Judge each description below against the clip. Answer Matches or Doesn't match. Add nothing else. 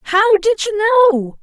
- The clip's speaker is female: Matches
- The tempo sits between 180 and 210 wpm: Doesn't match